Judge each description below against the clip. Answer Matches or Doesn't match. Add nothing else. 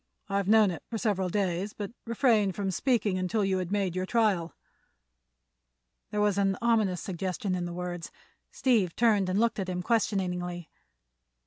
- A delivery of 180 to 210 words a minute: Doesn't match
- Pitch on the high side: Matches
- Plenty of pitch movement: Doesn't match